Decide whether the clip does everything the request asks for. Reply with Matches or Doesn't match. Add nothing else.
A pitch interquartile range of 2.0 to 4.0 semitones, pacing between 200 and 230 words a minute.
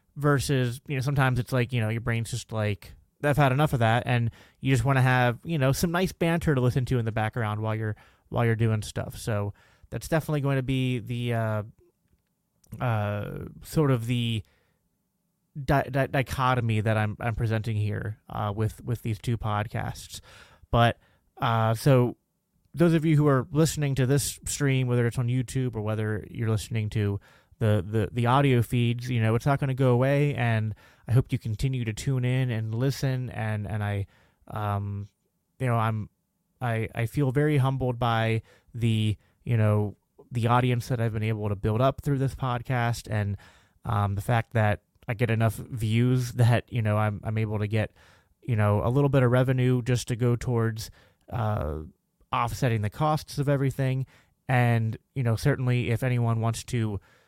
Doesn't match